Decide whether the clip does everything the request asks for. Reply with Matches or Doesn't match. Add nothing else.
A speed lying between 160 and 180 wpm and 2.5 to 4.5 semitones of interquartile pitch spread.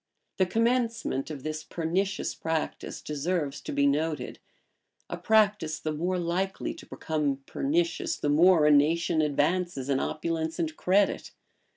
Doesn't match